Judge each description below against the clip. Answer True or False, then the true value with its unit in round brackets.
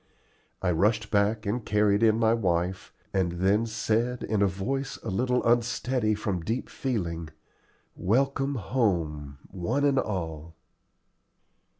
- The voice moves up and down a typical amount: True (4.6 semitones)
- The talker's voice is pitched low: True (105 Hz)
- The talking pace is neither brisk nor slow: False (125 wpm)